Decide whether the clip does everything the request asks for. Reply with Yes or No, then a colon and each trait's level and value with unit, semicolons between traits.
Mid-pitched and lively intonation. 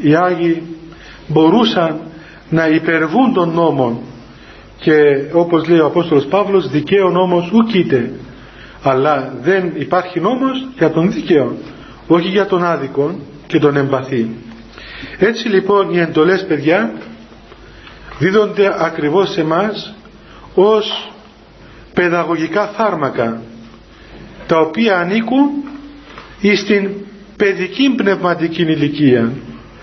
Yes: medium, 170 Hz; wide, 5.7 semitones